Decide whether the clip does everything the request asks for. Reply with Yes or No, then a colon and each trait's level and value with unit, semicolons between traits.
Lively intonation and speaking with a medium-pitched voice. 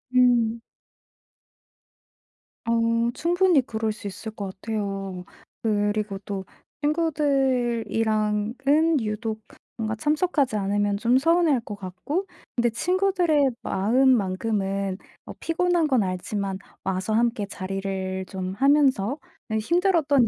No: wide, 5.8 semitones; high, 225 Hz